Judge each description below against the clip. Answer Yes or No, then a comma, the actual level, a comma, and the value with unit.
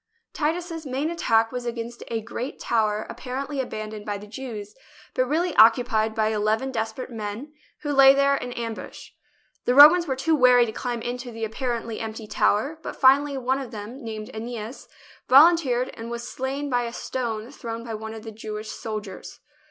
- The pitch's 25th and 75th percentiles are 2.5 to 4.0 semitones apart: Yes, average, 3.4 semitones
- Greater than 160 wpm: Yes, average, 185 wpm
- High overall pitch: Yes, high, 240 Hz